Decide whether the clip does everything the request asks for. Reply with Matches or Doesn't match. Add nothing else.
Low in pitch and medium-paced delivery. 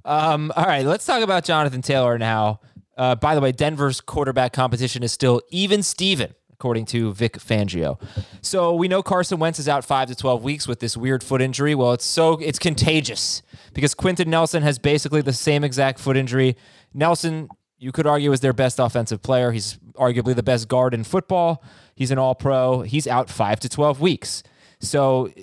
Matches